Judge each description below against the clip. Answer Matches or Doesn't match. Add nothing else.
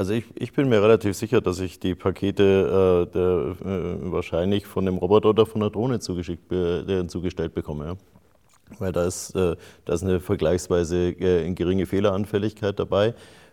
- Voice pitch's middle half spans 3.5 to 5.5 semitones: Doesn't match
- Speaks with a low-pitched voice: Matches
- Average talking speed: Matches